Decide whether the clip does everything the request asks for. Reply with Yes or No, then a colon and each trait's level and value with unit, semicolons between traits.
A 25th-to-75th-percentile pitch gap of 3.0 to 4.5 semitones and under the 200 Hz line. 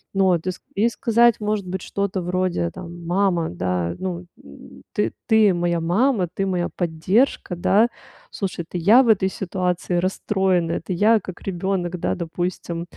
No: narrow, 2.4 semitones; medium, 185 Hz